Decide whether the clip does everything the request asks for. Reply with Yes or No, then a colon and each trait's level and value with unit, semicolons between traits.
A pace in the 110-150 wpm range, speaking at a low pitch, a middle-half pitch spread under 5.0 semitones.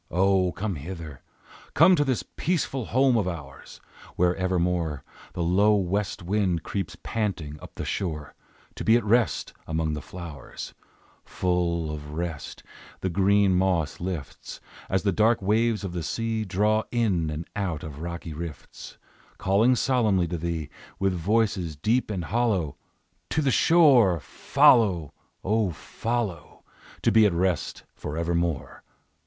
Yes: average, 140 wpm; very low, 90 Hz; average, 4.4 semitones